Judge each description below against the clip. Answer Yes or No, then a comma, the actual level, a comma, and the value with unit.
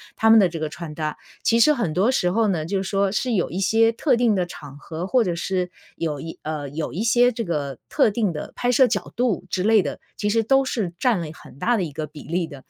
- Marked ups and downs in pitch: Yes, wide, 5.9 semitones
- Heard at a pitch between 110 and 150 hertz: No, high, 190 Hz